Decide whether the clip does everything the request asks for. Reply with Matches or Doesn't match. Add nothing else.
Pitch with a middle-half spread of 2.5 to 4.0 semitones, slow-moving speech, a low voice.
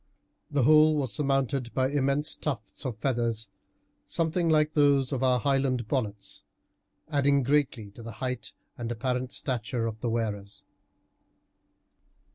Matches